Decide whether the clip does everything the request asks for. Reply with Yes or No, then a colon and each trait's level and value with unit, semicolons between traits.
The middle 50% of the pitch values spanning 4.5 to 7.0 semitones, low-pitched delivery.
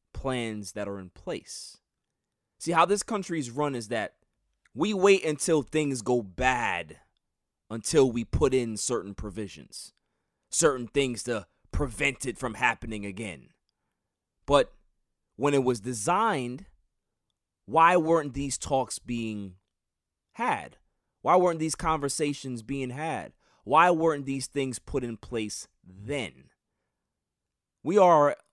Yes: average, 5.0 semitones; low, 125 Hz